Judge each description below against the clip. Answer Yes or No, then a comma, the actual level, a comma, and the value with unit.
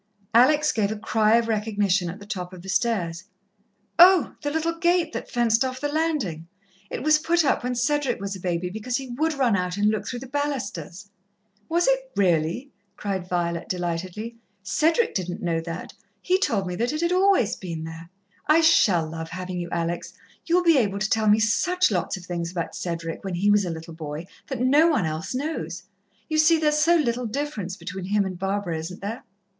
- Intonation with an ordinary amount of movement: No, wide, 8.3 semitones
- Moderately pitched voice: No, high, 210 Hz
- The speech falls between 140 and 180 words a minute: No, fast, 205 wpm